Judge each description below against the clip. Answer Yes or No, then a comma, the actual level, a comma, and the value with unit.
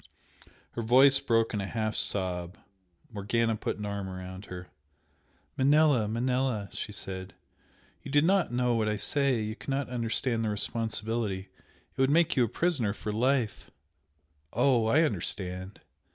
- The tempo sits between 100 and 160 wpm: Yes, average, 150 wpm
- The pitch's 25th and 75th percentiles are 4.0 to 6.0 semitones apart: Yes, average, 4.4 semitones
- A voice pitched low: Yes, low, 110 Hz